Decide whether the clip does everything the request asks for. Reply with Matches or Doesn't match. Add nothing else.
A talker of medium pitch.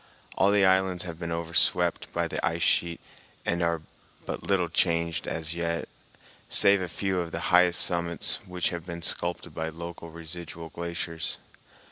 Doesn't match